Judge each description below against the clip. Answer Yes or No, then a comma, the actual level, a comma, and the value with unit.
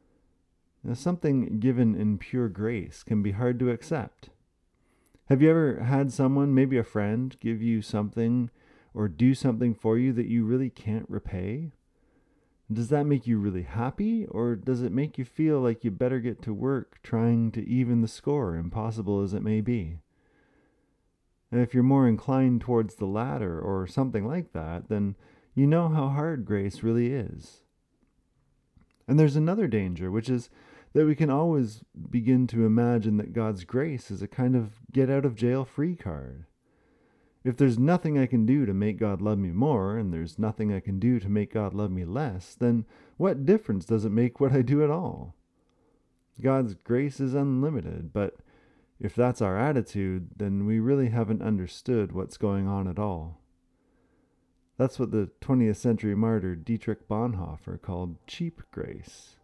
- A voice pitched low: Yes, low, 115 Hz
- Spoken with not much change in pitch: No, average, 4.2 semitones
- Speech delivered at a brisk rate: No, average, 175 wpm